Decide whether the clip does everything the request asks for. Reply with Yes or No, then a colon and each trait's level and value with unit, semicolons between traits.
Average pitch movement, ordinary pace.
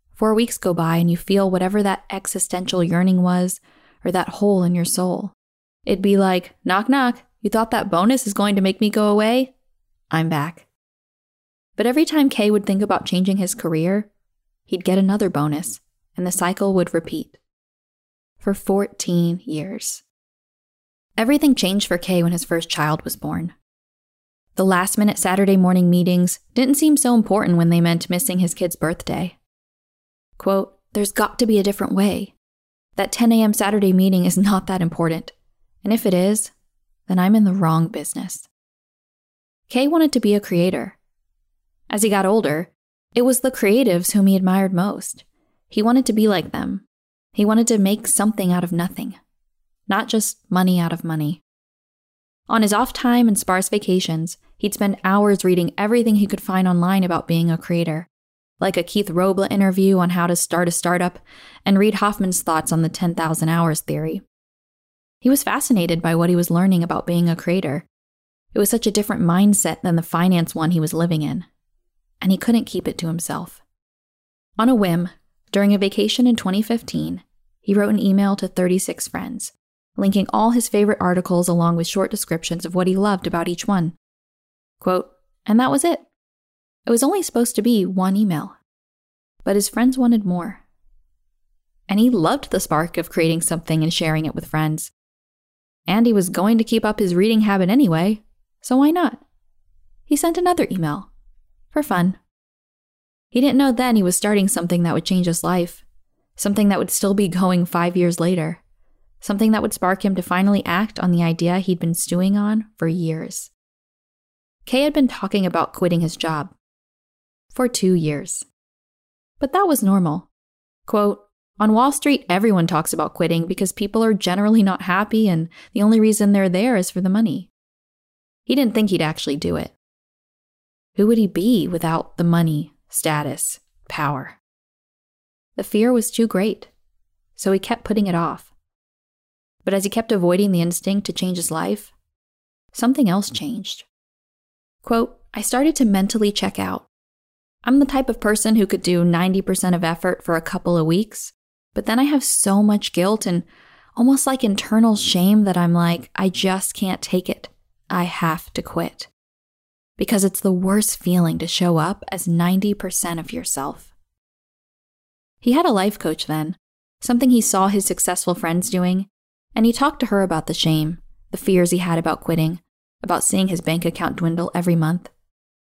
Yes: average, 3.8 semitones; average, 175 wpm